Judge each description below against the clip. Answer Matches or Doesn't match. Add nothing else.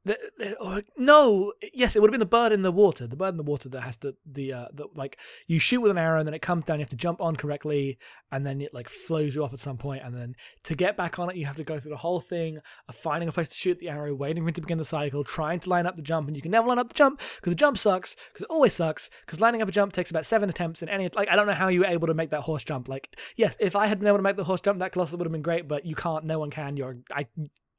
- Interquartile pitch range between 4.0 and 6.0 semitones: Matches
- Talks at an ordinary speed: Doesn't match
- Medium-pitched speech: Matches